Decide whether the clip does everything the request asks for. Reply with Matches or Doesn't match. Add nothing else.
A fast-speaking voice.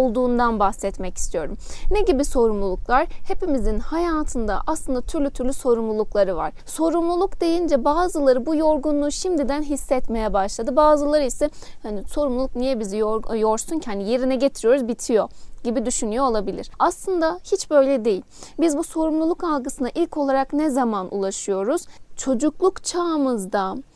Doesn't match